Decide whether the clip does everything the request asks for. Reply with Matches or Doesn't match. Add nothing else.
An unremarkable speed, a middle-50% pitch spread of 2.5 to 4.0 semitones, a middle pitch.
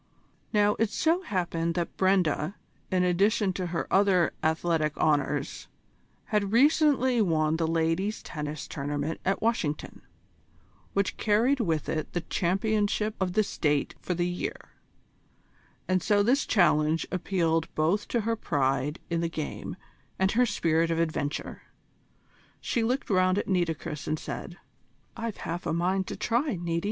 Doesn't match